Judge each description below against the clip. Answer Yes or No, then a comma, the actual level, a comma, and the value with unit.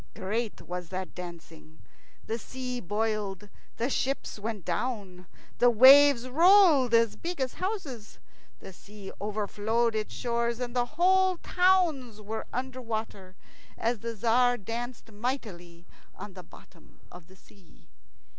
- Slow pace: Yes, slow, 130 wpm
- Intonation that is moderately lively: Yes, average, 4.0 semitones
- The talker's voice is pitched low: No, high, 230 Hz